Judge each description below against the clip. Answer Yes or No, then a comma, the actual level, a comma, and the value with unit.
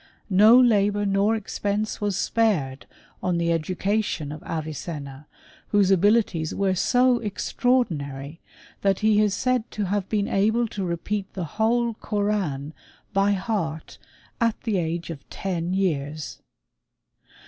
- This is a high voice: Yes, high, 195 Hz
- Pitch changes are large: No, average, 4.4 semitones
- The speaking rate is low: Yes, slow, 125 wpm